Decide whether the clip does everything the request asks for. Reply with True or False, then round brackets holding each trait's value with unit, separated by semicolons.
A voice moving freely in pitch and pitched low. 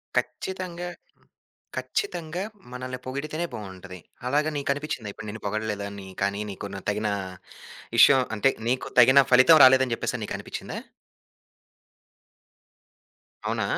True (6.5 semitones; 130 Hz)